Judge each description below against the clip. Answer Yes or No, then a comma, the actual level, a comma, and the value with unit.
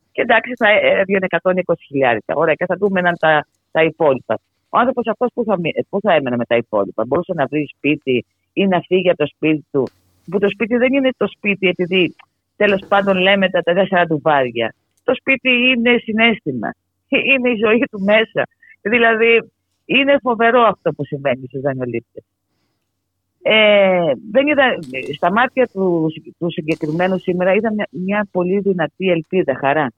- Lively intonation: Yes, wide, 7.3 semitones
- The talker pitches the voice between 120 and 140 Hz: No, medium, 185 Hz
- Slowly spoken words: No, average, 155 wpm